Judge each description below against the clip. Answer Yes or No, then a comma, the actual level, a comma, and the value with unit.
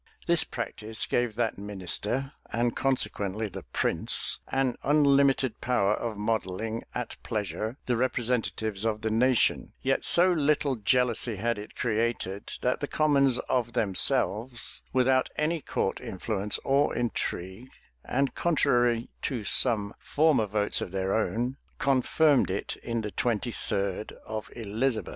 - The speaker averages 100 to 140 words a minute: Yes, slow, 135 wpm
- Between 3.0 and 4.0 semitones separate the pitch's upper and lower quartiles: Yes, average, 3.6 semitones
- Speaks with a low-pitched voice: Yes, low, 115 Hz